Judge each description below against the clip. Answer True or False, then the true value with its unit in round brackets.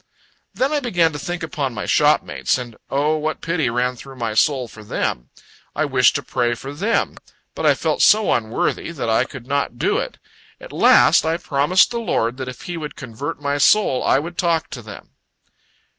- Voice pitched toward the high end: False (140 Hz)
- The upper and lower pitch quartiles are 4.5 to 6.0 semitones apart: True (5.2 semitones)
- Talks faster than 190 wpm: True (200 wpm)